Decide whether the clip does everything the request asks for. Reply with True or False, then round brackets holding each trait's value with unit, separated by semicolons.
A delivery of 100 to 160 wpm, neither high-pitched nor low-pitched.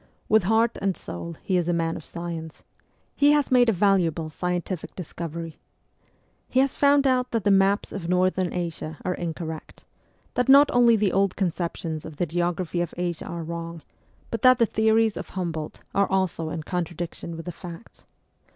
False (180 wpm; 180 Hz)